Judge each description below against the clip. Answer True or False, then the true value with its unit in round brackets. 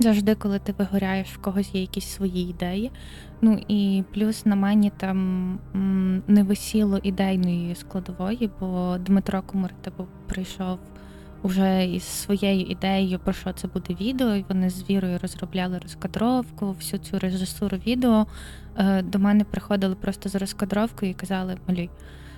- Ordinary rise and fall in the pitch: False (1.6 semitones)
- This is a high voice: True (195 Hz)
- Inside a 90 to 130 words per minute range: False (140 wpm)